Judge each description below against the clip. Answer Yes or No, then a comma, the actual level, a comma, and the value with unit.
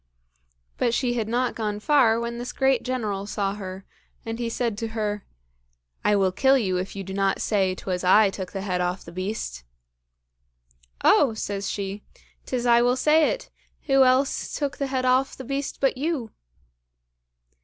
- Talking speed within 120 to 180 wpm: Yes, average, 175 wpm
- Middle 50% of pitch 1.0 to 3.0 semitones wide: No, average, 4.6 semitones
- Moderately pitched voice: No, high, 225 Hz